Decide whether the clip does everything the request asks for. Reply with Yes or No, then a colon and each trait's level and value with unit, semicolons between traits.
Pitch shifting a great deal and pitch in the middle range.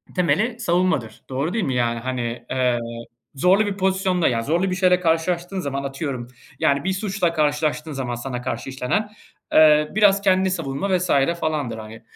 Yes: wide, 6.2 semitones; medium, 155 Hz